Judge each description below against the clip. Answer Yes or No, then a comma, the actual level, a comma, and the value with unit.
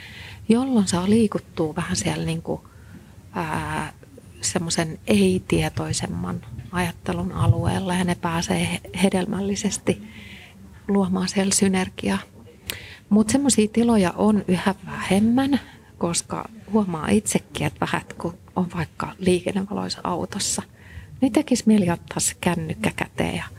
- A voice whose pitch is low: No, medium, 185 Hz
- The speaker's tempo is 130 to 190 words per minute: No, average, 100 wpm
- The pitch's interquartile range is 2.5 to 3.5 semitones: No, average, 4.0 semitones